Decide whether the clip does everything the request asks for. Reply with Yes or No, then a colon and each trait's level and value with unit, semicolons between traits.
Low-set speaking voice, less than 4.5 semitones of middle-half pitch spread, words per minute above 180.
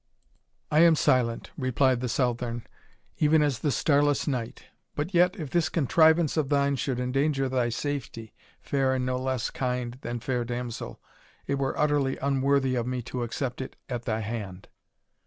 No: low, 130 Hz; average, 2.9 semitones; average, 165 wpm